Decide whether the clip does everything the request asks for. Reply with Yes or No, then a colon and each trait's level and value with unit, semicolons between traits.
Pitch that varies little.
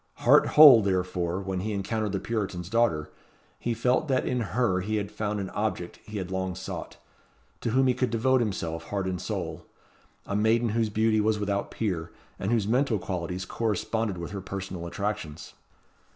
No: average, 3.5 semitones